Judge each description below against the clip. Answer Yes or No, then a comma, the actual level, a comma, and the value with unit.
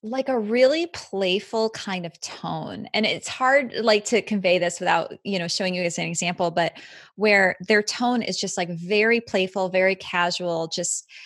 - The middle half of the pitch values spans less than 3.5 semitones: No, average, 3.8 semitones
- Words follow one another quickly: No, average, 180 wpm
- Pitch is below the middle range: No, high, 195 Hz